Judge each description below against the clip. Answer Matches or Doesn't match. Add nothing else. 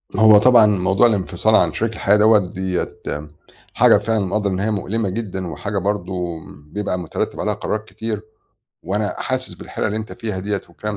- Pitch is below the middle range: Matches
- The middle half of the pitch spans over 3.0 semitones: Doesn't match